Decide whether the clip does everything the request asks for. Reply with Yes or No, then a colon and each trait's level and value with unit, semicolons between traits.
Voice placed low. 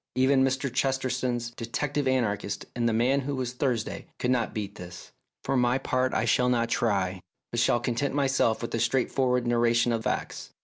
Yes: low, 125 Hz